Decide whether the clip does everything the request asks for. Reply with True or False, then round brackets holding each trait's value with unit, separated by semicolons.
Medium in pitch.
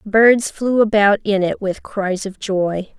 False (205 Hz)